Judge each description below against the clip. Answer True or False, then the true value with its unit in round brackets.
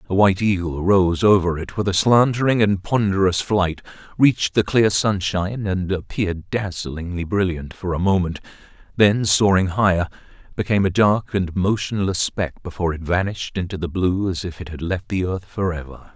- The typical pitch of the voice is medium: False (95 Hz)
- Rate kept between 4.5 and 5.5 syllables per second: True (5.1 syllables/s)